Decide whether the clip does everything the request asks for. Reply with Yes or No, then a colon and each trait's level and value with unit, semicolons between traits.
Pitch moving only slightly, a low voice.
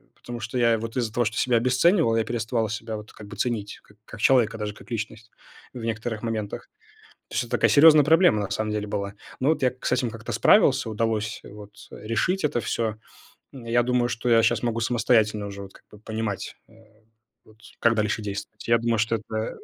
Yes: narrow, 2.0 semitones; low, 115 Hz